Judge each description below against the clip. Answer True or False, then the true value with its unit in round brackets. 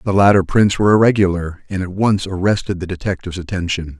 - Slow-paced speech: False (180 wpm)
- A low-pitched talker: True (95 Hz)